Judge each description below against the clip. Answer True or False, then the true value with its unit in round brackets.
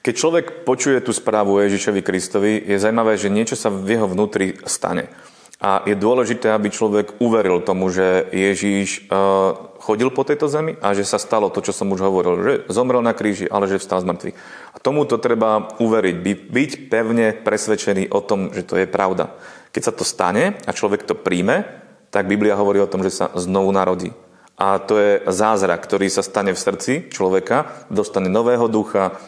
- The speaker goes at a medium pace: False (185 wpm)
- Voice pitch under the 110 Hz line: True (100 Hz)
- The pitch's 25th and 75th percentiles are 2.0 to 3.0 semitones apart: True (2.4 semitones)